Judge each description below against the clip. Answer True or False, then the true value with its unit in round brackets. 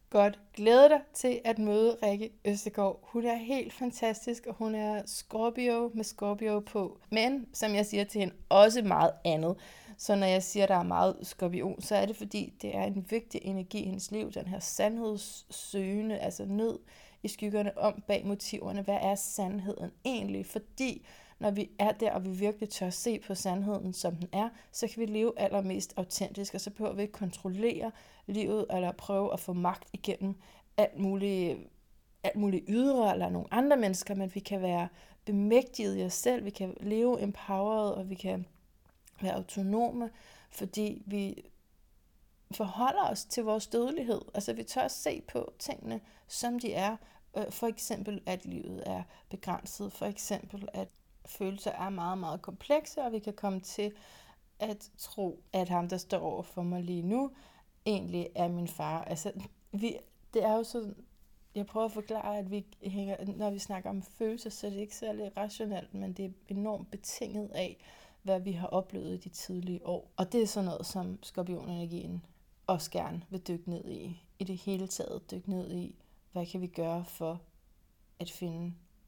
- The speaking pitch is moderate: False (200 Hz)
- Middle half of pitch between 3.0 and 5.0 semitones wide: False (2.5 semitones)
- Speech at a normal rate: True (180 wpm)